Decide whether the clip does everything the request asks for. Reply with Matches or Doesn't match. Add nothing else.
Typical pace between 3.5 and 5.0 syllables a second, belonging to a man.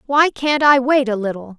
Doesn't match